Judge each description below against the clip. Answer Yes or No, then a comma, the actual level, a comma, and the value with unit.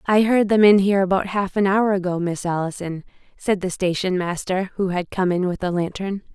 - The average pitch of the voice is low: No, high, 190 Hz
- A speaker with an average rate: No, fast, 220 wpm